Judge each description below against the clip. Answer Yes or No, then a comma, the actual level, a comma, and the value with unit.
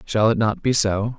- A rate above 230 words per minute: Yes, fast, 255 wpm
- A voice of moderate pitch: No, low, 115 Hz